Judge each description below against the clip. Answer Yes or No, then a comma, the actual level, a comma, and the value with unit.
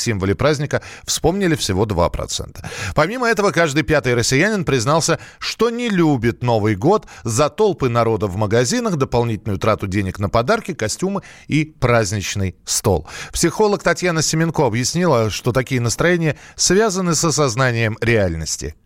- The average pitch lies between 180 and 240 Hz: No, low, 130 Hz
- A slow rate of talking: No, average, 130 wpm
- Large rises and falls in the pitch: Yes, wide, 7.2 semitones